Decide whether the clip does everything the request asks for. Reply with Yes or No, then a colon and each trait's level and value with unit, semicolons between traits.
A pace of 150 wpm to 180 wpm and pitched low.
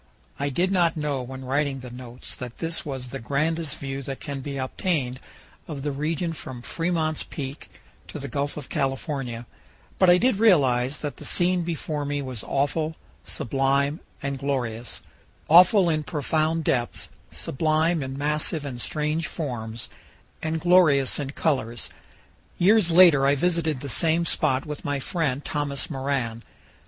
No: average, 155 wpm; medium, 145 Hz